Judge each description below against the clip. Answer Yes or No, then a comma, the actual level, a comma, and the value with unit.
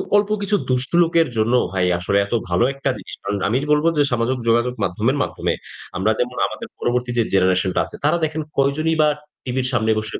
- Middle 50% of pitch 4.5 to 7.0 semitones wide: Yes, wide, 5.4 semitones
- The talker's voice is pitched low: Yes, low, 125 Hz